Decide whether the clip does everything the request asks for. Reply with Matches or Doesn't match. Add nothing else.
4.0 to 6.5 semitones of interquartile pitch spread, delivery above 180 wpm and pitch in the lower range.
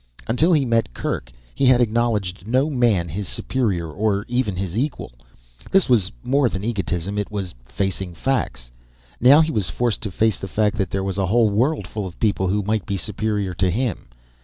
Matches